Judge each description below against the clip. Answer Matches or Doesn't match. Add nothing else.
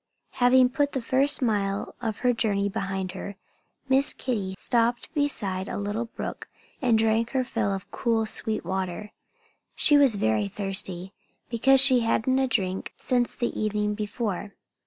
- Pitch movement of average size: Matches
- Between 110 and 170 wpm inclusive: Matches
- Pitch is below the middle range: Doesn't match